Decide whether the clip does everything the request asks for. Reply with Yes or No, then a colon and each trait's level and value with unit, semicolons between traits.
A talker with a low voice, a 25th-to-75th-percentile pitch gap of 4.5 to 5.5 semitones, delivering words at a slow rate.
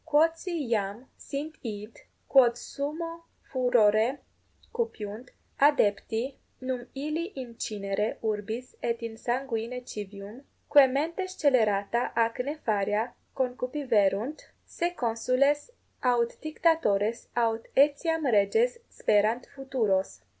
No: high, 245 Hz; average, 4.8 semitones; slow, 95 wpm